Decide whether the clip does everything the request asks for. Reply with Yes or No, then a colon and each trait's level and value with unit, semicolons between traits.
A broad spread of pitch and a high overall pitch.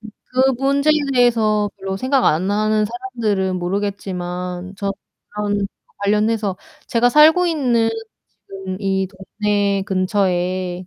No: average, 3.2 semitones; high, 205 Hz